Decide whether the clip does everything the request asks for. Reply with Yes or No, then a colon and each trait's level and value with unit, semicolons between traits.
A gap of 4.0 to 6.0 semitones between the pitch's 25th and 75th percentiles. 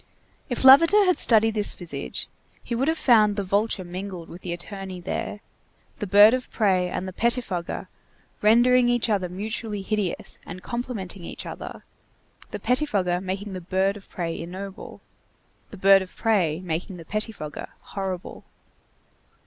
No: average, 3.5 semitones